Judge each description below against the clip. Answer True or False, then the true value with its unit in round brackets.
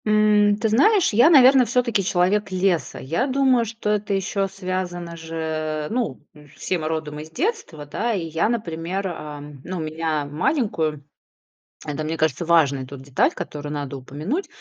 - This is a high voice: False (175 Hz)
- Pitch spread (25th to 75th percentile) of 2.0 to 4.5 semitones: False (5.5 semitones)